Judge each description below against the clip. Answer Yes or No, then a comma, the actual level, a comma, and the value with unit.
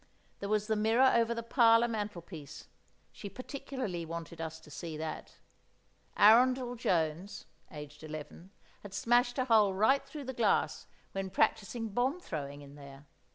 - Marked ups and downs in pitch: Yes, wide, 6.8 semitones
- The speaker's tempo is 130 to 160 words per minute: Yes, average, 150 wpm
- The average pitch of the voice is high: Yes, high, 205 Hz